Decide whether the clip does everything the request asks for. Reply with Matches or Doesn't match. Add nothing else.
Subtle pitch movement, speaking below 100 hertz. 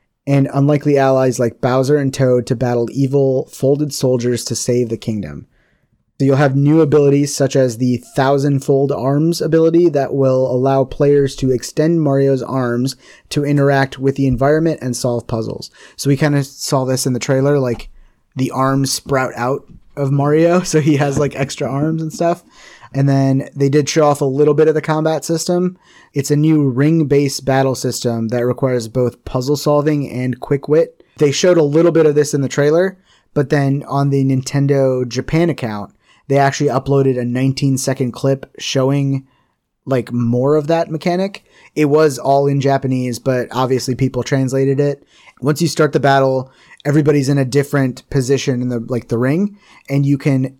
Doesn't match